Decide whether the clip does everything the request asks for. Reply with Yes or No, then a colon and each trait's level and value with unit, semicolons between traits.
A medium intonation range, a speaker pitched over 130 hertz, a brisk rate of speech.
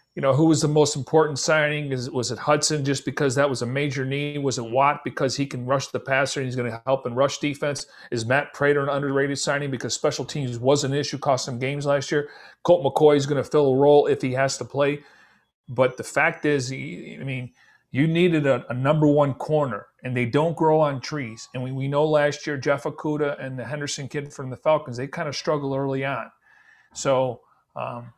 No: narrow, 2.0 semitones; medium, 140 Hz; fast, 230 wpm